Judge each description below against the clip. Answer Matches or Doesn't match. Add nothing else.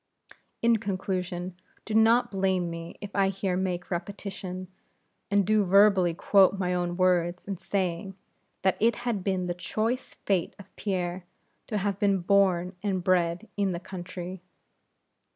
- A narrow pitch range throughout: Matches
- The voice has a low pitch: Doesn't match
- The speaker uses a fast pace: Doesn't match